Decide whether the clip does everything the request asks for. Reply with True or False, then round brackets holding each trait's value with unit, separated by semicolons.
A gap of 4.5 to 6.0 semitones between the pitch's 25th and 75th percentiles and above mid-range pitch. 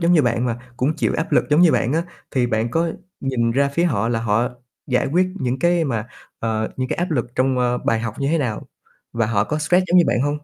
False (5.4 semitones; 130 Hz)